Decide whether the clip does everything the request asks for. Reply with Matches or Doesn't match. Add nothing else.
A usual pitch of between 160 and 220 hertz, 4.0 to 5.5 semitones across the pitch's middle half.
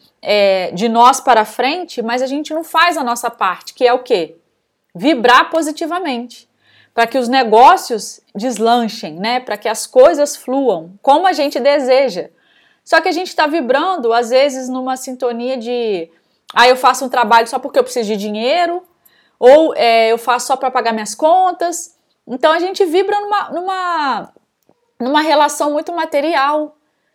Doesn't match